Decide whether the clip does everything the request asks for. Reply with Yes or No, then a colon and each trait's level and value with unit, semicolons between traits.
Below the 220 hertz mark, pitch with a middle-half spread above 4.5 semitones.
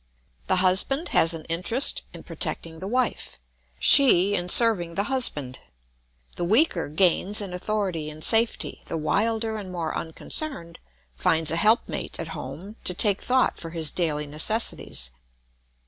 Yes: medium, 185 Hz; average, 5.2 semitones